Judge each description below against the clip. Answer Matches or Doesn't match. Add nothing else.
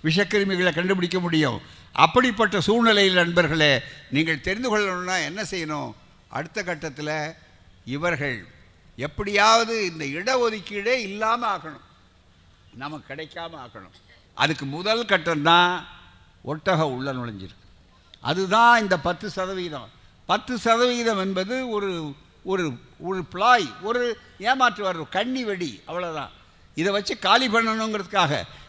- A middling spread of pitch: Doesn't match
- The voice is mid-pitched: Matches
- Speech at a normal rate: Matches